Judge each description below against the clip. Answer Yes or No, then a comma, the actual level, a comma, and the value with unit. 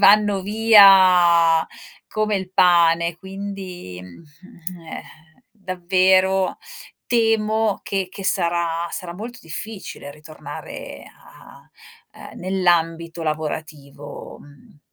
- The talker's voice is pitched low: No, medium, 180 Hz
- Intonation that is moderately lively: Yes, average, 3.1 semitones